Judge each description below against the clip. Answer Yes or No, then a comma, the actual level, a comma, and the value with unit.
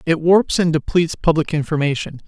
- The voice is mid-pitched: Yes, medium, 160 Hz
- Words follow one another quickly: No, average, 160 wpm